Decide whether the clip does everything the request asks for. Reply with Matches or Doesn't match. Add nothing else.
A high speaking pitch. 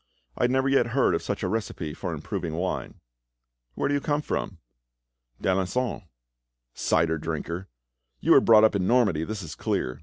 Doesn't match